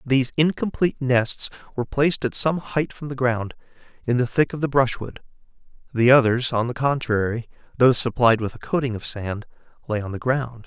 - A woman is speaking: No, male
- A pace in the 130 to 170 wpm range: No, average, 185 wpm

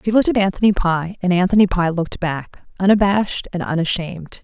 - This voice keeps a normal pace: Yes, average, 175 wpm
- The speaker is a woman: Yes, female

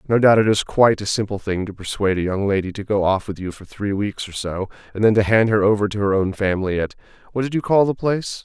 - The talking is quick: Yes, fast, 275 wpm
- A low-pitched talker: Yes, low, 105 Hz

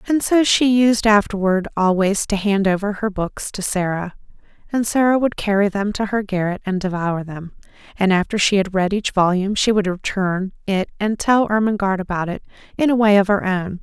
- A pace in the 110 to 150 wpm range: No, average, 200 wpm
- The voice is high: Yes, high, 200 Hz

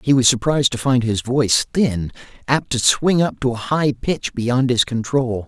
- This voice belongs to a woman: No, male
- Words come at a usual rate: No, fast, 210 wpm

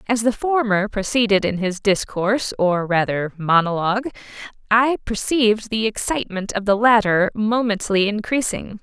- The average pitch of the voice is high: Yes, high, 210 Hz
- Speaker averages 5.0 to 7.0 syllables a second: No, 4.8 syllables/s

